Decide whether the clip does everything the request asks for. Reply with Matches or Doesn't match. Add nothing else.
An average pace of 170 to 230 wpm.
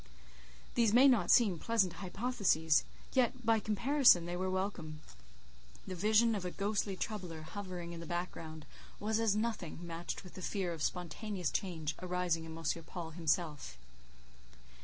Doesn't match